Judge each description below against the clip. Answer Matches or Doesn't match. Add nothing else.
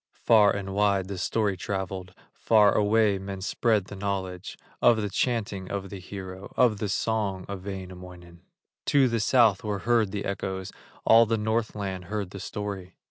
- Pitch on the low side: Matches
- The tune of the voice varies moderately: Doesn't match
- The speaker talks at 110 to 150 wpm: Doesn't match